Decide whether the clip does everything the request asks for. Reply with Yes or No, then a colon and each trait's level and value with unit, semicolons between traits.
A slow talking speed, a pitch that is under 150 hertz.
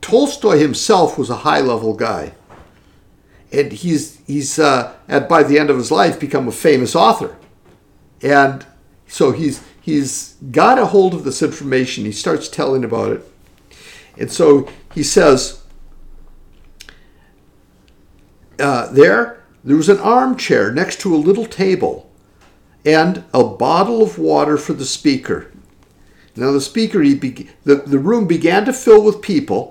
No: average, 145 wpm; medium, 140 Hz